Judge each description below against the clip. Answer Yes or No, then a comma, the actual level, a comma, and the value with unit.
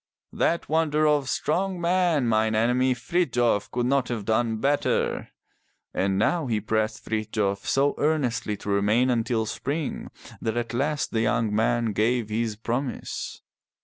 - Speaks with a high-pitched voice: No, low, 120 Hz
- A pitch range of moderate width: Yes, average, 4.5 semitones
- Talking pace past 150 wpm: No, average, 145 wpm